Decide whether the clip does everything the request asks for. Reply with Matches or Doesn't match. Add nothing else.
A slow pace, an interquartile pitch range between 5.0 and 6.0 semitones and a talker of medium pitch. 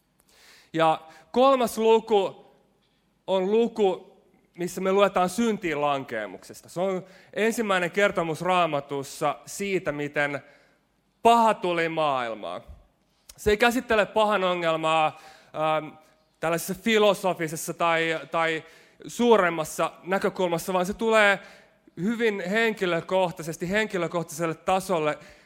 Doesn't match